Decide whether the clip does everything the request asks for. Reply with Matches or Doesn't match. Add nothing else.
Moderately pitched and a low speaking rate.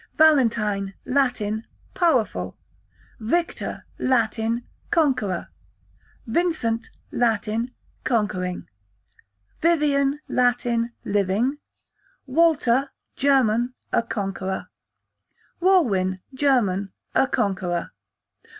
Doesn't match